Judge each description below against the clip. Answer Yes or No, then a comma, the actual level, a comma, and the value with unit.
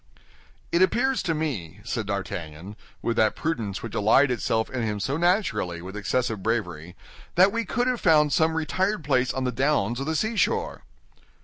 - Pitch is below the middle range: Yes, low, 130 Hz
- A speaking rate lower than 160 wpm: No, average, 175 wpm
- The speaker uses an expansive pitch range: Yes, wide, 7.8 semitones